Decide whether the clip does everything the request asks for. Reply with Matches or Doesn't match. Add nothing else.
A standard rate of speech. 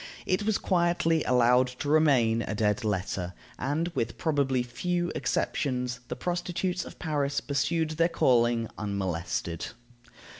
Doesn't match